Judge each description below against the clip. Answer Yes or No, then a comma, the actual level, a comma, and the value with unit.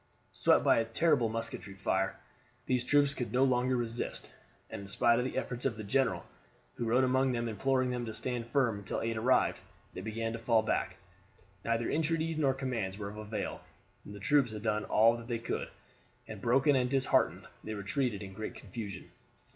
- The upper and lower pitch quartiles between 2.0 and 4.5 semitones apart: Yes, average, 3.2 semitones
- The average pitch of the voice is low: Yes, low, 115 Hz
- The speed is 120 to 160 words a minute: No, average, 190 wpm